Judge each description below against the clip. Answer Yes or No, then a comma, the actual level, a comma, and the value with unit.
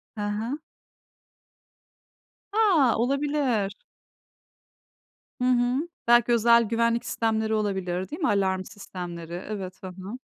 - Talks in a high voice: Yes, high, 225 Hz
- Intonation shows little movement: No, average, 4.0 semitones